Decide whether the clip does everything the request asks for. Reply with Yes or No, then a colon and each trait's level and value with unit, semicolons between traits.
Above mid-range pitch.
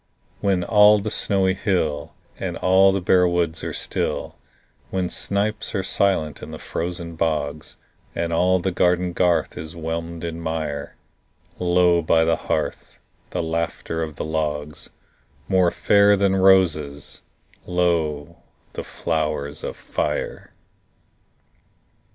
No: very low, 85 Hz